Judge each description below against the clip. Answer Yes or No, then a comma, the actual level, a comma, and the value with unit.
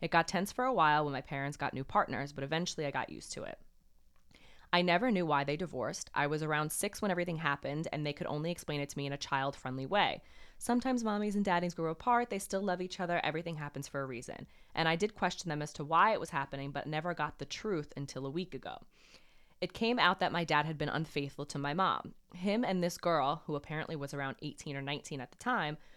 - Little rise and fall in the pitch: No, average, 4.0 semitones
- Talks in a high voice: No, medium, 155 Hz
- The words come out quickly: Yes, fast, 245 wpm